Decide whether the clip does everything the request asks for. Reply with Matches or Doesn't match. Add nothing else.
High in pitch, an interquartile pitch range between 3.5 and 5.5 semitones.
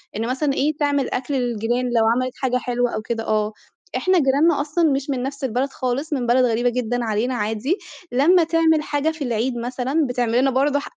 Doesn't match